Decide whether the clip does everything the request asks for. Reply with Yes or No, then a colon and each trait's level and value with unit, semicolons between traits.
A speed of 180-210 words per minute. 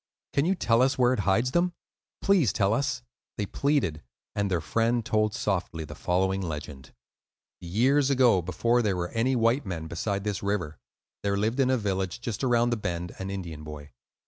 Yes: average, 185 wpm